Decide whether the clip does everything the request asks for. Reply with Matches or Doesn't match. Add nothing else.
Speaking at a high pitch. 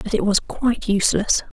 Matches